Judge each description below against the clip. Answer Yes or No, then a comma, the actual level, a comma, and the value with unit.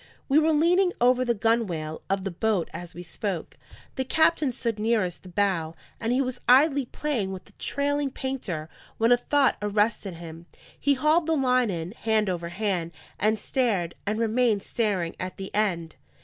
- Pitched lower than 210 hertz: No, high, 220 Hz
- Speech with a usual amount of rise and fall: No, wide, 5.9 semitones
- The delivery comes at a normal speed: Yes, average, 175 wpm